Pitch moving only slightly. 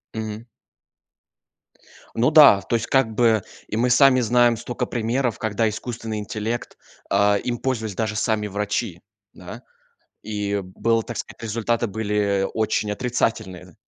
Yes: narrow, 2.2 semitones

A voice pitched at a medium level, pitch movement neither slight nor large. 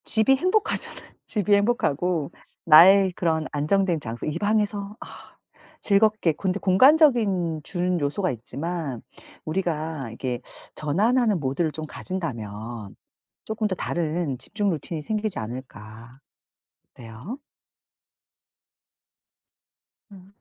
No: medium, 175 Hz; wide, 6.2 semitones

